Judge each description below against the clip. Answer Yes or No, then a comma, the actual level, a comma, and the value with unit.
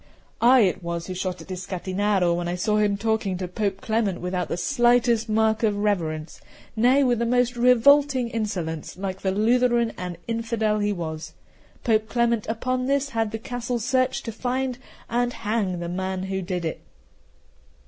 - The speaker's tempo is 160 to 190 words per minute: Yes, average, 170 wpm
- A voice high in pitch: Yes, high, 215 Hz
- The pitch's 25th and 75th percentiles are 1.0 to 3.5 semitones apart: No, average, 4.4 semitones